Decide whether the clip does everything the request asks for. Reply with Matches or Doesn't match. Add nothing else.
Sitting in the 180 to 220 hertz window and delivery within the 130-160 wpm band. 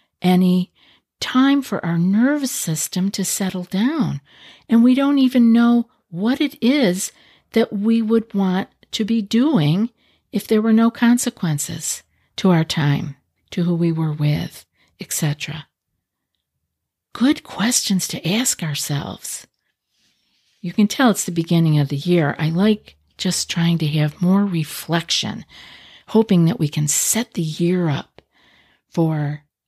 Matches